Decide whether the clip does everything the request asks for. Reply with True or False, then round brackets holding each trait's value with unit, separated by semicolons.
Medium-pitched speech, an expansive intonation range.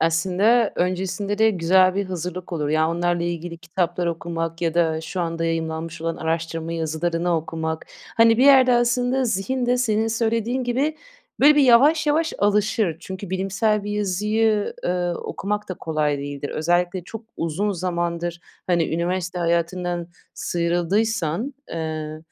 False (180 Hz; 4.4 semitones)